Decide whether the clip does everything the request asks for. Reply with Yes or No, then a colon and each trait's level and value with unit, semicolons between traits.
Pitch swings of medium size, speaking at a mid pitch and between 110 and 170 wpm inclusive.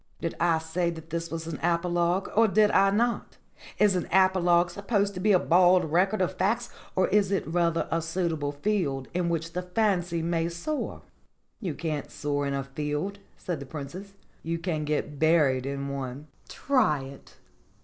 No: average, 3.7 semitones; medium, 170 Hz; average, 180 wpm